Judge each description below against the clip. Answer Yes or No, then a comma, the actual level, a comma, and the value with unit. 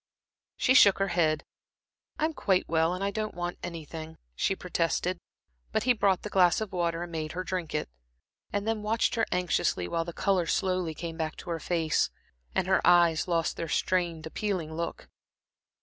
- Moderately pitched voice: Yes, medium, 175 Hz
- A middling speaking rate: Yes, average, 180 wpm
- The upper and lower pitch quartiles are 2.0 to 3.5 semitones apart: Yes, average, 2.8 semitones